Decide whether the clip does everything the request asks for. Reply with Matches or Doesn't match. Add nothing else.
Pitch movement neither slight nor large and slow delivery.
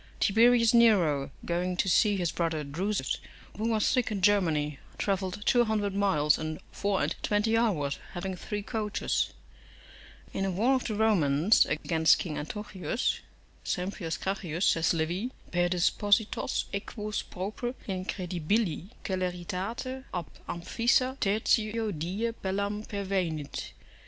Matches